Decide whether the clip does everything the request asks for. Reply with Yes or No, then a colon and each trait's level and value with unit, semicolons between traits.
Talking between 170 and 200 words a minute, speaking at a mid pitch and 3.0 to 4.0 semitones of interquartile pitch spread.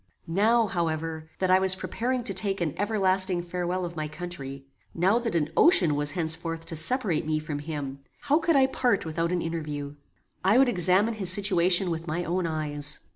Yes: average, 185 wpm; medium, 175 Hz; average, 3.7 semitones